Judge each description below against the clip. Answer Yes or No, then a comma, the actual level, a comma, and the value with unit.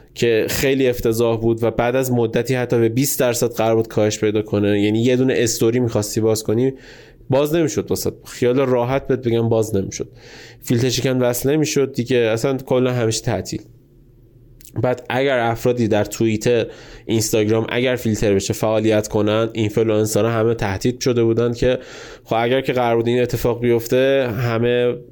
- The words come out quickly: Yes, fast, 160 wpm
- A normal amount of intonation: No, narrow, 2.1 semitones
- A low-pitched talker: Yes, low, 120 Hz